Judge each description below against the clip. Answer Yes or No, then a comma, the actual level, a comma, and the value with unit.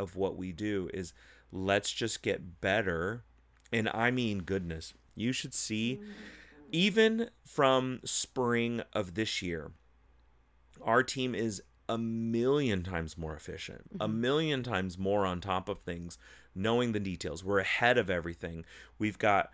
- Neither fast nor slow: Yes, average, 145 wpm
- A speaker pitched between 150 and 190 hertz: No, low, 100 Hz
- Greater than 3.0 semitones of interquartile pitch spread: Yes, wide, 5.5 semitones